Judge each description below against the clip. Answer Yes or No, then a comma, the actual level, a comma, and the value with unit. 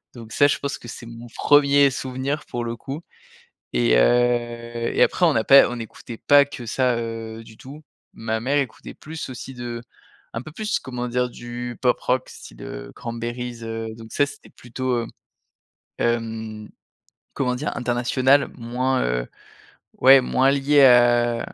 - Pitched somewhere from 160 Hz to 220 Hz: No, low, 120 Hz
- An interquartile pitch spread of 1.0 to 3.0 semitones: Yes, narrow, 2.4 semitones